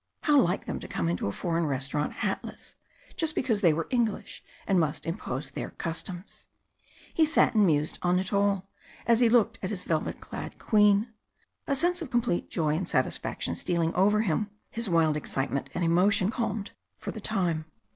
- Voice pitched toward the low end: No, high, 190 Hz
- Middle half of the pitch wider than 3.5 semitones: Yes, average, 5.3 semitones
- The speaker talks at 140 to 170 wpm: No, average, 180 wpm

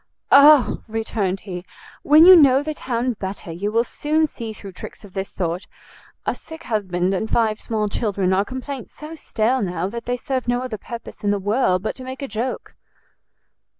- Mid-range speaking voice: No, high, 225 Hz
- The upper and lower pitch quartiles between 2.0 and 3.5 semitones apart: No, average, 4.8 semitones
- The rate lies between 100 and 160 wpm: No, average, 190 wpm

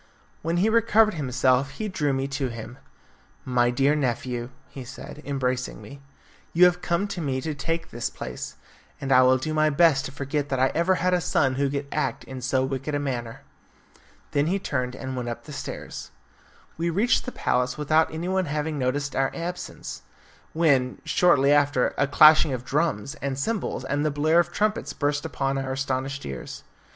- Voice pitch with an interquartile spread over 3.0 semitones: Yes, average, 3.7 semitones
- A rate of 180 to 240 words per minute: Yes, average, 185 wpm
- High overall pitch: No, medium, 140 Hz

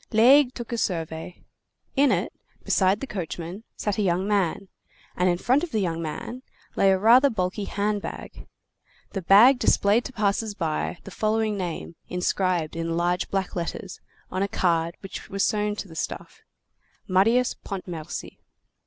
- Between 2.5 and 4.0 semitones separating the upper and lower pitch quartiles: Yes, average, 3.7 semitones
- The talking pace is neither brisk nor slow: Yes, average, 160 wpm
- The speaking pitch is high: Yes, high, 195 Hz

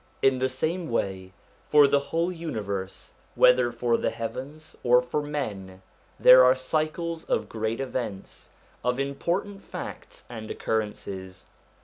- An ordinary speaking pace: No, slow, 130 wpm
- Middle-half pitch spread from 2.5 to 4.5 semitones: No, wide, 5.4 semitones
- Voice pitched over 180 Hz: No, low, 130 Hz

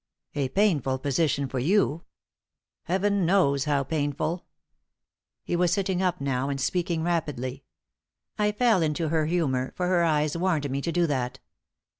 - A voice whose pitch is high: No, medium, 160 Hz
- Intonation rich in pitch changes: No, average, 4.3 semitones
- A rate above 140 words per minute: Yes, average, 150 wpm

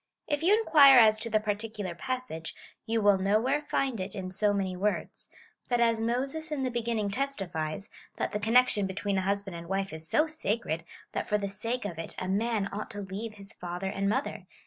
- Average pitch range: Yes, average, 3.9 semitones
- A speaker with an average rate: No, fast, 210 wpm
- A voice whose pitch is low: No, high, 210 Hz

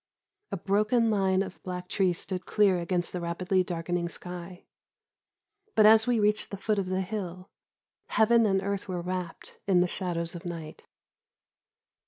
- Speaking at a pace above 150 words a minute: Yes, average, 160 wpm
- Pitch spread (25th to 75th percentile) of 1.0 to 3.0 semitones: Yes, narrow, 2.4 semitones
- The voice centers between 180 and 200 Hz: Yes, medium, 185 Hz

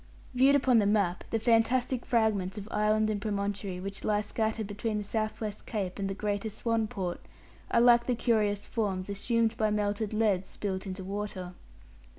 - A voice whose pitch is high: Yes, high, 210 Hz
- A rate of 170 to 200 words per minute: Yes, average, 175 wpm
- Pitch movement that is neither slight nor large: No, narrow, 2.1 semitones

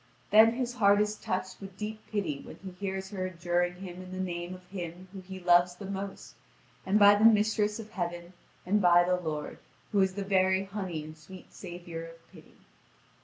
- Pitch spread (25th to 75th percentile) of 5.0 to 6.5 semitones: No, narrow, 2.4 semitones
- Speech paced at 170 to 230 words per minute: Yes, average, 200 wpm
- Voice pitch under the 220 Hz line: Yes, medium, 185 Hz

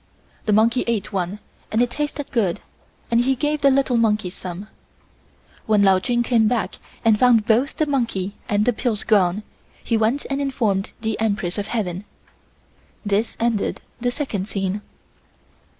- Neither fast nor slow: Yes, average, 160 wpm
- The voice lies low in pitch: No, high, 220 Hz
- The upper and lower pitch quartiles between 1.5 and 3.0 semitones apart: No, average, 3.4 semitones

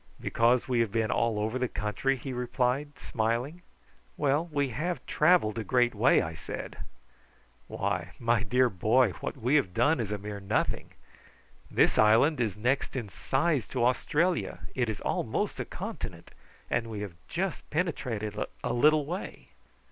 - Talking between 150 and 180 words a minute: Yes, average, 160 wpm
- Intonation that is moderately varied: Yes, average, 4.5 semitones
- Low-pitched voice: Yes, low, 125 Hz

